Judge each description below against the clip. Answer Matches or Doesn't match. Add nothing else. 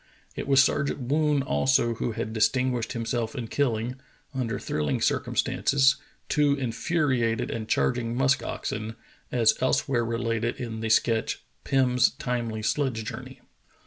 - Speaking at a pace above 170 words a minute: Doesn't match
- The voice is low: Matches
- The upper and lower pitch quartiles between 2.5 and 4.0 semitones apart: Matches